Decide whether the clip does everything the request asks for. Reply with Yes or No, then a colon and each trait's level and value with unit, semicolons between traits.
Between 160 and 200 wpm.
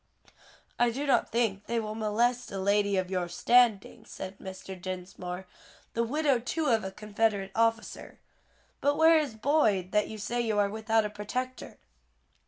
Yes: average, 165 wpm